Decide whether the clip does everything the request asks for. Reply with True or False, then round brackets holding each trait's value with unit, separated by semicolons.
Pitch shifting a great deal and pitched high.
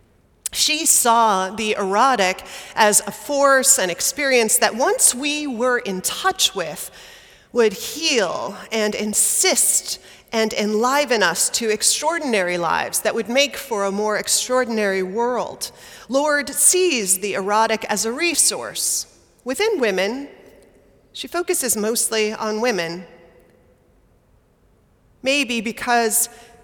False (4.4 semitones; 230 Hz)